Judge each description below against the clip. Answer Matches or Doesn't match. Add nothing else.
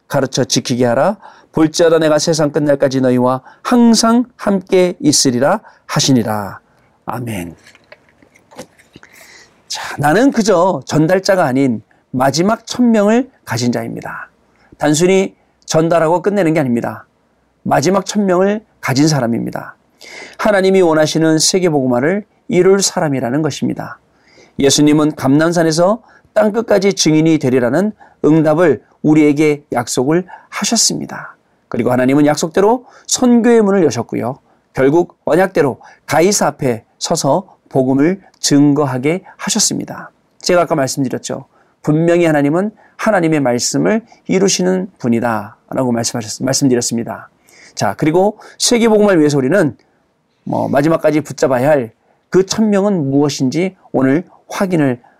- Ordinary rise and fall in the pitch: Doesn't match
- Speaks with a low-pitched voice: Doesn't match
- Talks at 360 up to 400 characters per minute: Doesn't match